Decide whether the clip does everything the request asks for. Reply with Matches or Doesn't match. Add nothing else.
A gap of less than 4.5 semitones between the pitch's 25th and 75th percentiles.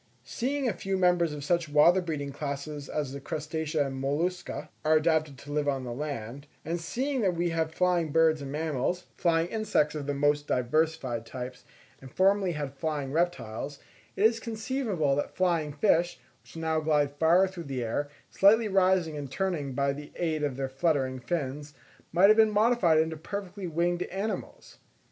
Matches